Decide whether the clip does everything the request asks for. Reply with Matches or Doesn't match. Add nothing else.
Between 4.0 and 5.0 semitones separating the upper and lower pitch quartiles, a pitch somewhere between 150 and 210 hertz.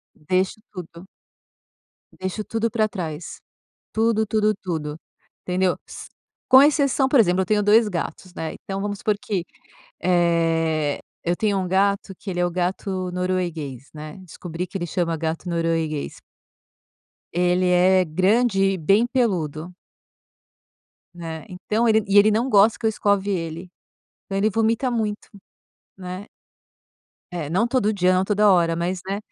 Doesn't match